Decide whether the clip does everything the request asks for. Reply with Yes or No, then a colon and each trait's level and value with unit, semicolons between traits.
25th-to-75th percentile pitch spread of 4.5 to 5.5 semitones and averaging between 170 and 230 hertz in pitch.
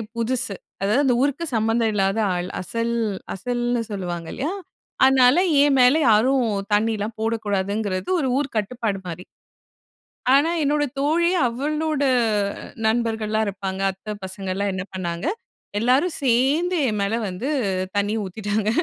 Yes: average, 4.8 semitones; high, 225 Hz